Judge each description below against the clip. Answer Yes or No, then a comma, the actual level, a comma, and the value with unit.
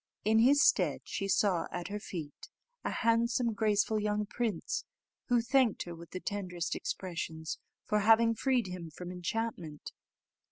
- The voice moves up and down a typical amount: Yes, average, 4.4 semitones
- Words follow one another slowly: No, average, 150 wpm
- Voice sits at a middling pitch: No, high, 205 Hz